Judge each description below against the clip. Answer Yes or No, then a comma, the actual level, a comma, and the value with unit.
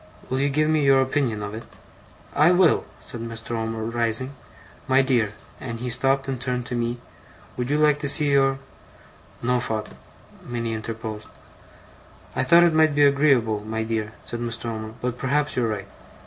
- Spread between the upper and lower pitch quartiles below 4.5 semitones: Yes, average, 3.7 semitones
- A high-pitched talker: No, low, 125 Hz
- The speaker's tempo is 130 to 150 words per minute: No, average, 180 wpm